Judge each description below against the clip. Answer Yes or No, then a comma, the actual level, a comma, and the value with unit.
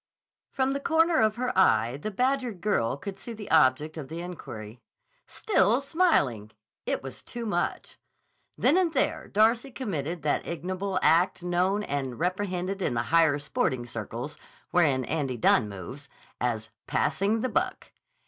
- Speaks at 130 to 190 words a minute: Yes, average, 150 wpm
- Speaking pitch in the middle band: Yes, medium, 175 Hz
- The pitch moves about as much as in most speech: No, wide, 8.5 semitones